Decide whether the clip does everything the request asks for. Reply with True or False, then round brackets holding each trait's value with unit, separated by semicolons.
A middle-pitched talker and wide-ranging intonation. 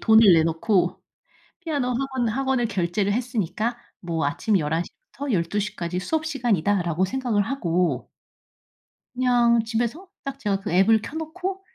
False (220 Hz; 6.3 semitones)